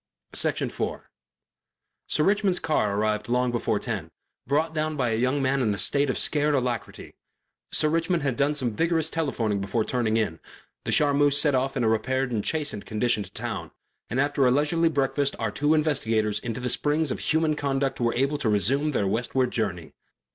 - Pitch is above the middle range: No, low, 135 Hz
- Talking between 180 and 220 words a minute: Yes, average, 190 wpm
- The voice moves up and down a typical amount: Yes, average, 4.6 semitones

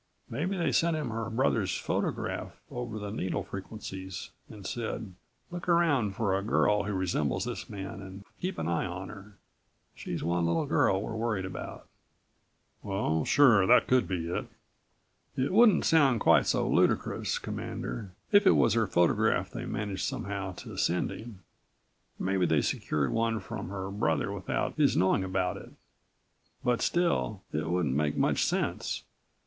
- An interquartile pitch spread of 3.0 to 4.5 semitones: Yes, average, 3.9 semitones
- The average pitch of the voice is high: No, low, 100 Hz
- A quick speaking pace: No, average, 160 wpm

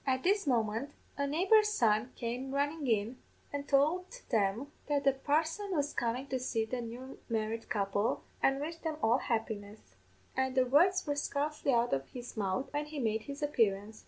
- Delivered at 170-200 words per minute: Yes, average, 180 wpm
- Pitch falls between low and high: No, very high, 260 Hz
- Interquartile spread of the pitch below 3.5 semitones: No, average, 4.6 semitones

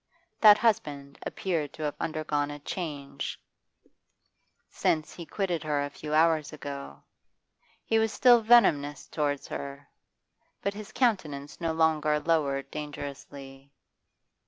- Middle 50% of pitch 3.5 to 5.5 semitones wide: No, average, 2.9 semitones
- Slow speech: Yes, slow, 120 wpm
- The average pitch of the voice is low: No, medium, 150 Hz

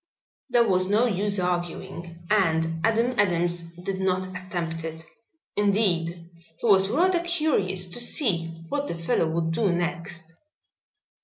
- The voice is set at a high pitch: No, medium, 180 Hz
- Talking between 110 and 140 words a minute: Yes, slow, 135 wpm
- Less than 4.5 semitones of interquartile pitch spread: Yes, average, 3.8 semitones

